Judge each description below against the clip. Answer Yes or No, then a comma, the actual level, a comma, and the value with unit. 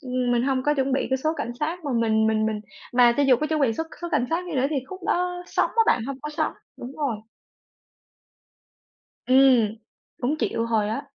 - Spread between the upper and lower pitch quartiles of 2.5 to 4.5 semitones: Yes, average, 4.2 semitones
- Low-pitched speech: No, very high, 265 Hz